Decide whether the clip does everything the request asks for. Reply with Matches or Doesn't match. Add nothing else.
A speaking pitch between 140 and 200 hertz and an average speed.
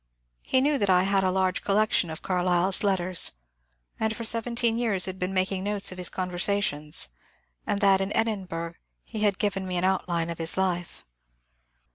Matches